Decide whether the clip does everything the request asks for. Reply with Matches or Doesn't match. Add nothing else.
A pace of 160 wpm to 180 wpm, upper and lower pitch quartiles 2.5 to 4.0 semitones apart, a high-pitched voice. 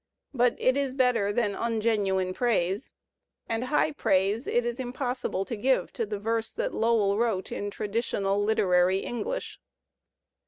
Doesn't match